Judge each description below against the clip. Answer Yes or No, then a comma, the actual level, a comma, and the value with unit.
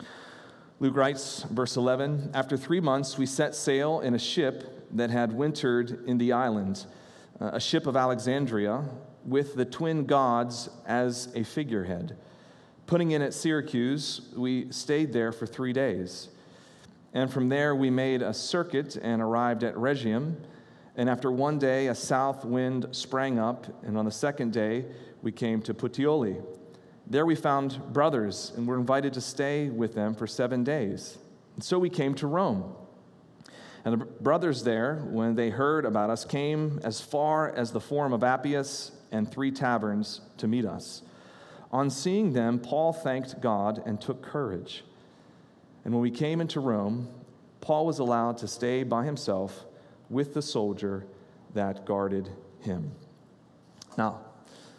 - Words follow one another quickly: No, average, 155 wpm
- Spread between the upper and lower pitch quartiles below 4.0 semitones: Yes, average, 3.6 semitones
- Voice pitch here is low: Yes, low, 125 Hz